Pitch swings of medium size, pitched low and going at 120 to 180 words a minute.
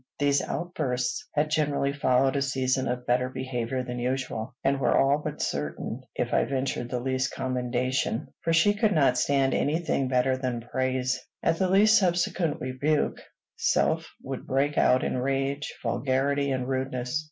No: narrow, 2.2 semitones; low, 130 Hz; average, 160 wpm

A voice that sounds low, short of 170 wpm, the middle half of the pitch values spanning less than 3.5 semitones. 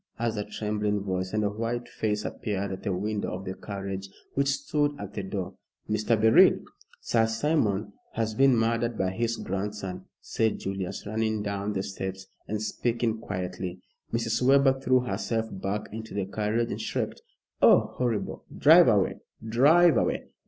Yes: low, 105 Hz; average, 160 wpm; average, 3.0 semitones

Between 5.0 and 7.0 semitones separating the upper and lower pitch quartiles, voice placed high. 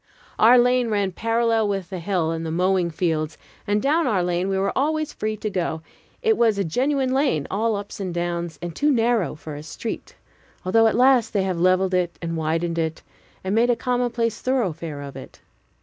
Yes: wide, 5.5 semitones; high, 195 Hz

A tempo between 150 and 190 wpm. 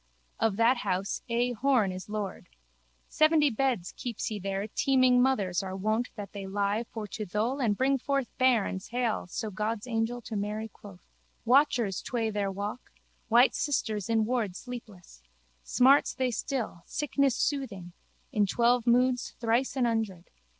Yes: average, 155 wpm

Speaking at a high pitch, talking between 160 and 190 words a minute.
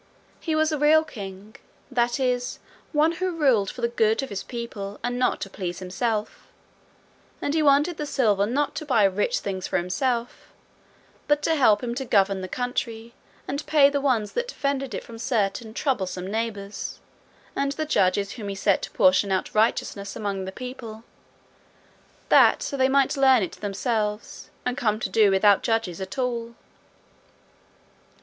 Yes: high, 235 Hz; average, 170 wpm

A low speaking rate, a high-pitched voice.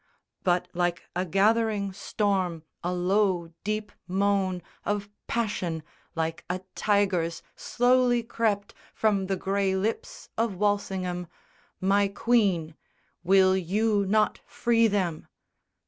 Yes: slow, 110 wpm; high, 195 Hz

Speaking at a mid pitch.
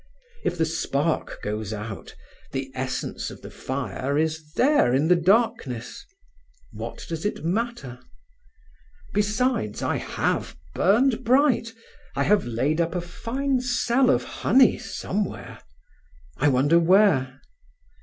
Yes: medium, 165 Hz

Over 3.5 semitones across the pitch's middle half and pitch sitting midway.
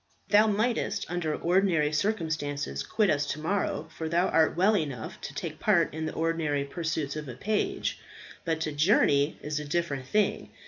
Yes: average, 4.1 semitones; medium, 160 Hz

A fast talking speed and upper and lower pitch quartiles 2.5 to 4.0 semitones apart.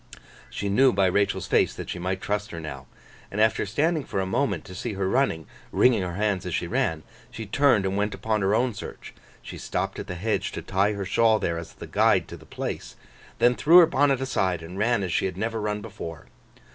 Yes: fast, 230 wpm; average, 3.7 semitones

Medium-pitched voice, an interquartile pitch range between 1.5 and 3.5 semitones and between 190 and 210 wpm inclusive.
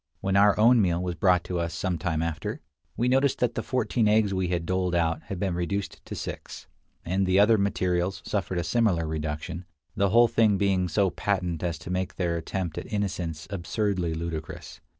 No: very low, 90 Hz; average, 3.1 semitones; average, 195 wpm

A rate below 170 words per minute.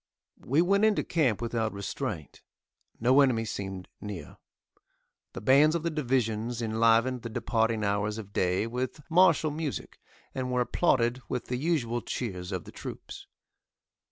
Yes: average, 145 wpm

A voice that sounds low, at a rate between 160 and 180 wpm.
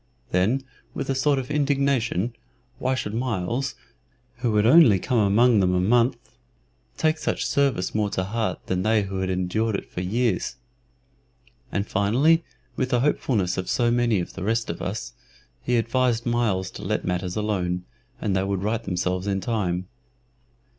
Yes: low, 110 Hz; average, 165 wpm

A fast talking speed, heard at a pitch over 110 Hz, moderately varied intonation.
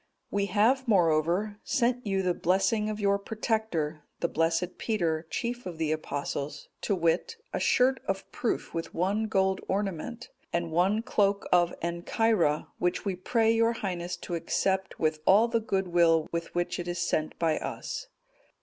No: average, 160 wpm; high, 190 Hz; average, 4.4 semitones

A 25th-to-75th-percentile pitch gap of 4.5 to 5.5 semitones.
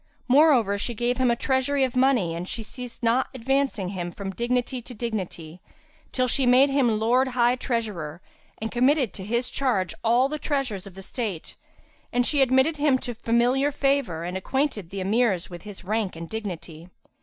Yes: average, 5.1 semitones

